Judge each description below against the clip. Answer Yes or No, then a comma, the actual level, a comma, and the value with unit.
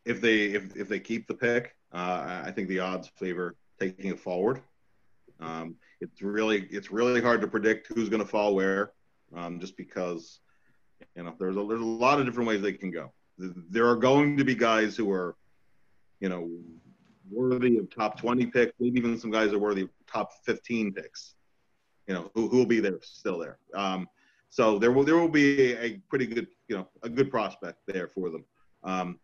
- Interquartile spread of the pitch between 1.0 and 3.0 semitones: No, average, 4.2 semitones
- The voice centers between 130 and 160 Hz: No, low, 105 Hz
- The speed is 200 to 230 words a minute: Yes, fast, 205 wpm